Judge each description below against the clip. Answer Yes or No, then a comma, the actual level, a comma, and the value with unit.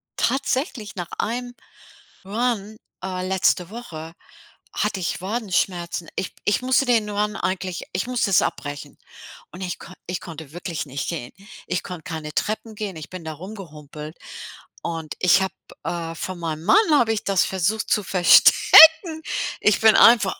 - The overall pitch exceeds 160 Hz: Yes, high, 190 Hz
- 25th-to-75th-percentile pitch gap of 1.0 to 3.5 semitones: No, average, 4.5 semitones